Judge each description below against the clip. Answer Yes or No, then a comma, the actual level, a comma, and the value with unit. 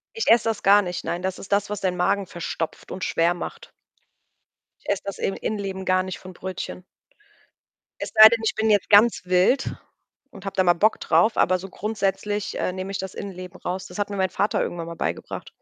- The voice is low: No, high, 190 Hz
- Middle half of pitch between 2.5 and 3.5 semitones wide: No, narrow, 2.0 semitones